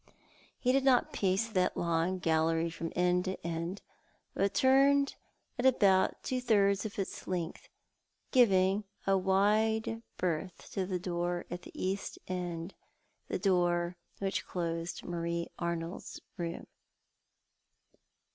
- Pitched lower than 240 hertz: Yes, medium, 185 Hz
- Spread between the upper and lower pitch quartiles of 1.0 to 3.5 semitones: Yes, average, 2.8 semitones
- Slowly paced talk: Yes, slow, 125 wpm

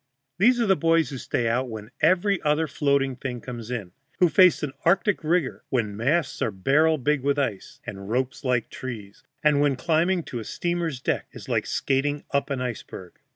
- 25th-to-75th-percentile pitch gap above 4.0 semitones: Yes, average, 4.8 semitones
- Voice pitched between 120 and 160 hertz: Yes, medium, 140 Hz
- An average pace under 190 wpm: No, average, 195 wpm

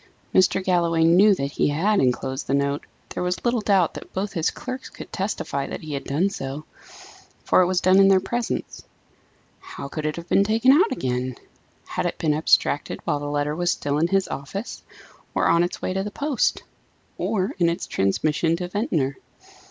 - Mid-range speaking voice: Yes, medium, 170 Hz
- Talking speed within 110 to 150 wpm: No, average, 195 wpm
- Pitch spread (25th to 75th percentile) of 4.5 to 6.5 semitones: Yes, average, 5.1 semitones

